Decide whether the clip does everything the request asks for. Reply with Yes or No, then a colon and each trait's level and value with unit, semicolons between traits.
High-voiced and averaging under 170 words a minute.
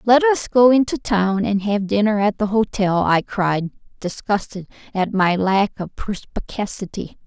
Yes: high, 205 Hz; average, 155 wpm